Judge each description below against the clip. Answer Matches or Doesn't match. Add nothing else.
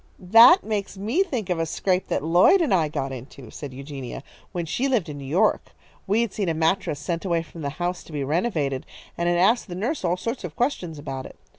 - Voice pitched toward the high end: Doesn't match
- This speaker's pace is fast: Matches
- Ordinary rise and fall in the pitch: Doesn't match